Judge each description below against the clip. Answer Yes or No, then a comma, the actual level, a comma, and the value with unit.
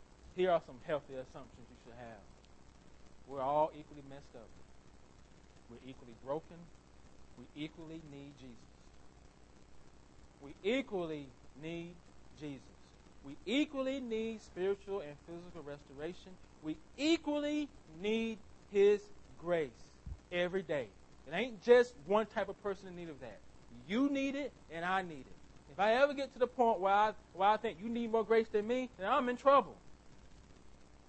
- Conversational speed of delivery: Yes, average, 150 wpm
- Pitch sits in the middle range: Yes, medium, 170 Hz